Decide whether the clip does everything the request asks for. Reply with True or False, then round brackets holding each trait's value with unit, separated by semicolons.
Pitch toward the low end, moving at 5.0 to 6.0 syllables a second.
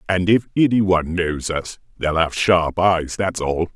False (90 Hz; 4.3 syllables/s)